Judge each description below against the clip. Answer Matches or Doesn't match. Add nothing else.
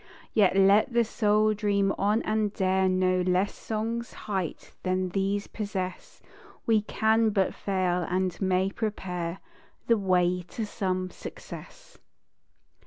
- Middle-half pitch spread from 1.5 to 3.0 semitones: Matches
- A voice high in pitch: Matches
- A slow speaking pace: Matches